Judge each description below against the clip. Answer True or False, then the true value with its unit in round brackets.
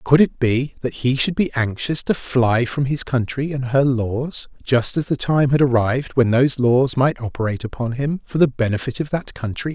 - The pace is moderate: False (215 wpm)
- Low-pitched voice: True (130 Hz)